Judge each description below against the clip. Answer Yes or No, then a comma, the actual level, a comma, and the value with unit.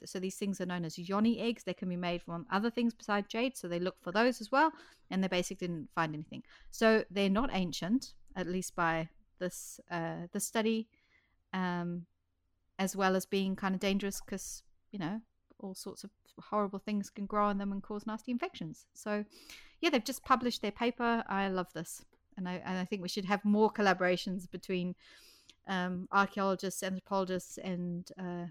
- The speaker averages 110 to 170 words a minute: No, average, 190 wpm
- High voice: Yes, high, 195 Hz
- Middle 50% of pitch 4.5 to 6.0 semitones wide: No, average, 3.1 semitones